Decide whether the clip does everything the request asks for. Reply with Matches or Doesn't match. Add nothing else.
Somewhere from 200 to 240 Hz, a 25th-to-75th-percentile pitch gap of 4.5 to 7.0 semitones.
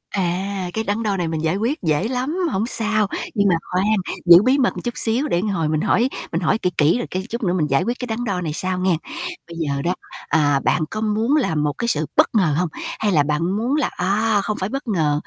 Doesn't match